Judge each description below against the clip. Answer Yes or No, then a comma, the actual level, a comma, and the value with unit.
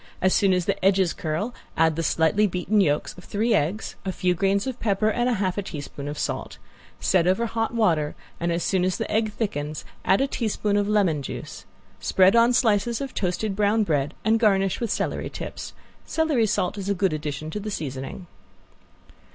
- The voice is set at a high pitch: Yes, high, 195 Hz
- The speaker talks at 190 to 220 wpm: Yes, average, 195 wpm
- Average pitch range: Yes, average, 4.3 semitones